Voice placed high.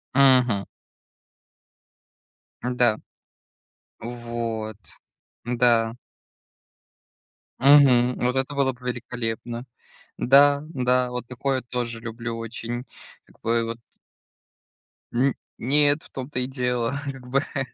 No: low, 125 Hz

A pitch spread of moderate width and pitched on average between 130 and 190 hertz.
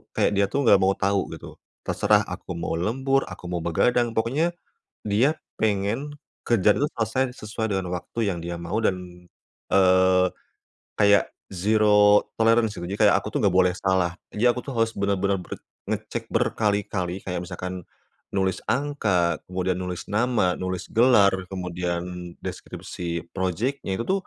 No: average, 3.7 semitones; low, 100 Hz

